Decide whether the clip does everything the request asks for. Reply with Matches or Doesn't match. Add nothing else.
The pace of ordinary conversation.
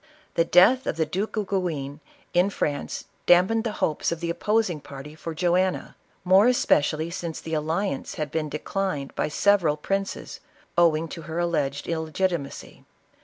Matches